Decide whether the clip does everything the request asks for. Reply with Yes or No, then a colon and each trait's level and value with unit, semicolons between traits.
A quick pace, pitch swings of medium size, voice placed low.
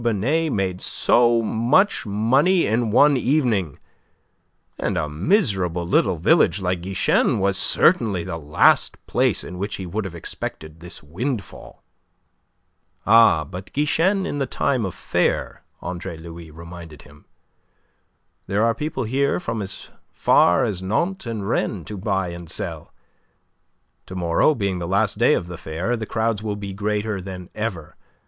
No: average, 150 wpm; average, 4.8 semitones; low, 100 Hz